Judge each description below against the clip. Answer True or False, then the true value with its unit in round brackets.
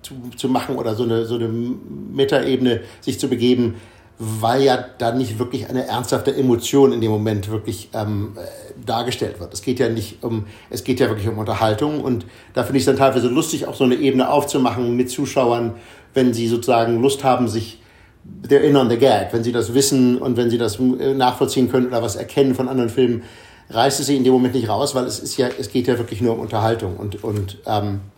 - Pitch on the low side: True (120 Hz)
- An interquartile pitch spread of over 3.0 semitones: False (2.5 semitones)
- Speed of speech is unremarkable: False (215 wpm)